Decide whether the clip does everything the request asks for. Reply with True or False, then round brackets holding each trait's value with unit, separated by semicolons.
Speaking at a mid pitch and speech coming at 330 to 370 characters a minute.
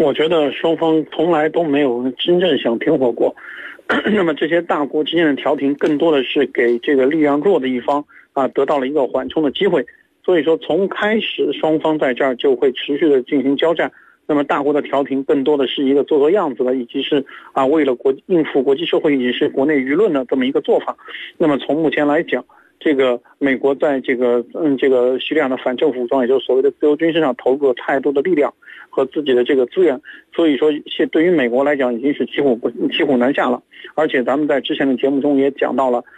True (145 Hz; 340 characters per minute)